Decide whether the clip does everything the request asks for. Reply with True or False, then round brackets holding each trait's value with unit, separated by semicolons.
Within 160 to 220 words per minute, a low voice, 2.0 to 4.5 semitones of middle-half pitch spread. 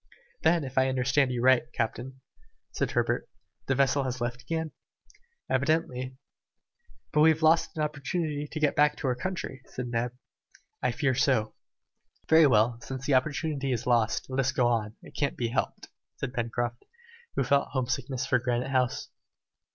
True (170 wpm; 130 Hz; 2.9 semitones)